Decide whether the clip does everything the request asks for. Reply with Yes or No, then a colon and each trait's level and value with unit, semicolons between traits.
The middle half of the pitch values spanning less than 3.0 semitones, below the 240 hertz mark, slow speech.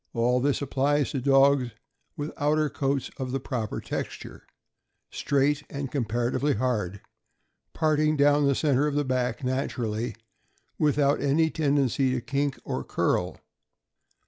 Yes: narrow, 2.5 semitones; medium, 140 Hz; slow, 130 wpm